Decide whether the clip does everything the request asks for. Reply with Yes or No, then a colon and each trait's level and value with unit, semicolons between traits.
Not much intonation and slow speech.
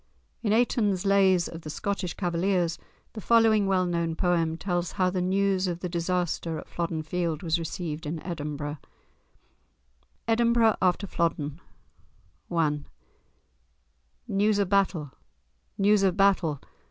No: average, 3.2 semitones; slow, 130 wpm